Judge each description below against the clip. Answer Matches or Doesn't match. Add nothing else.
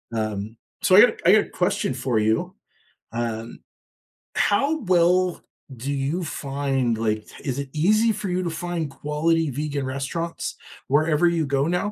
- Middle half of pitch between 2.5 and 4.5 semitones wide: Doesn't match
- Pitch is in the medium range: Matches